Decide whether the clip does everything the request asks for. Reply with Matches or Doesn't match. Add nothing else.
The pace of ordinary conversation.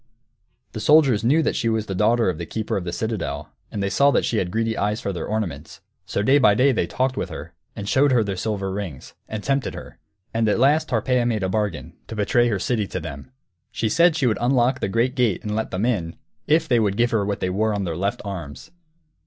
Doesn't match